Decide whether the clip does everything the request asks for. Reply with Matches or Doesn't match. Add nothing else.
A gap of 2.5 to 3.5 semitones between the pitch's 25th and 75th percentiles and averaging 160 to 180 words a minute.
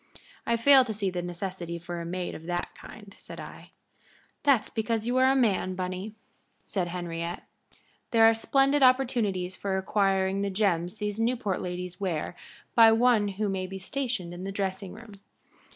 Doesn't match